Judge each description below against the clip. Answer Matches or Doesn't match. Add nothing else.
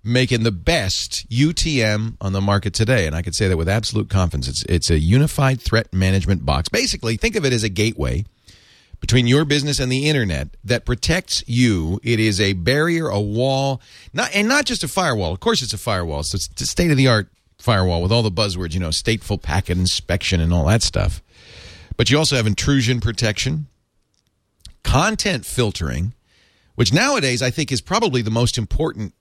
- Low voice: Matches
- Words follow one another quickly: Doesn't match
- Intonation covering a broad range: Matches